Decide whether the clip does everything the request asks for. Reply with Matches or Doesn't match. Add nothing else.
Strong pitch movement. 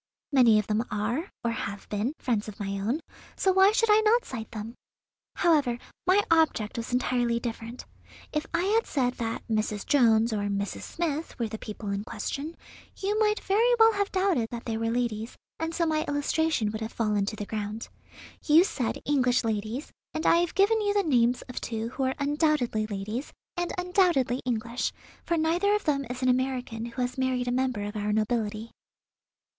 Matches